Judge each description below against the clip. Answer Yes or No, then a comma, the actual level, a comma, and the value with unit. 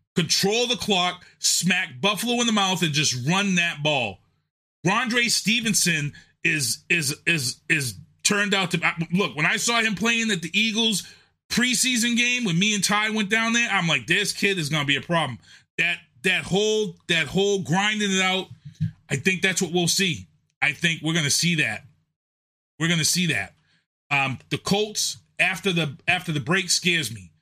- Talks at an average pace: Yes, average, 180 wpm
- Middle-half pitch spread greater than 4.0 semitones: Yes, average, 4.8 semitones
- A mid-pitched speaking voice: Yes, medium, 175 Hz